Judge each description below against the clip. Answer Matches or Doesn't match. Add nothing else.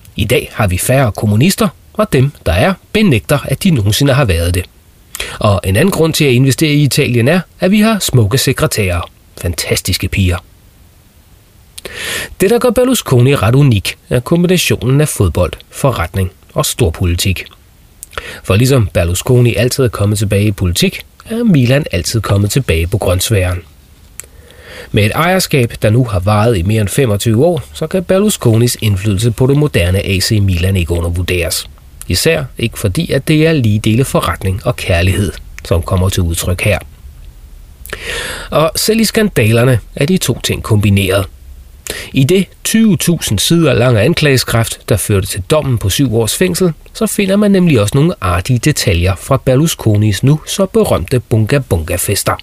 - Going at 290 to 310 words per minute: Doesn't match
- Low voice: Matches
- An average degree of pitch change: Doesn't match